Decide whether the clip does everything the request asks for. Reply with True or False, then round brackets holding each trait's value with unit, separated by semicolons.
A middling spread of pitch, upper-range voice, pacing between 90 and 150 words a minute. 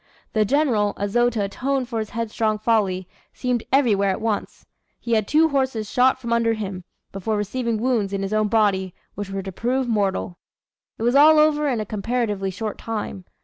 False (3.6 semitones; 220 Hz; 190 wpm)